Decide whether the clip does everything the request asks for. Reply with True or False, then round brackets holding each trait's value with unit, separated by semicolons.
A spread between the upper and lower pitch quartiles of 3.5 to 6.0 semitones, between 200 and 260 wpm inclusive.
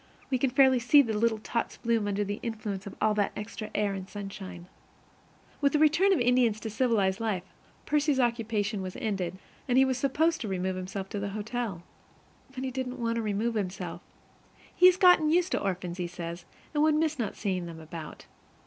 True (5.0 semitones; 205 wpm)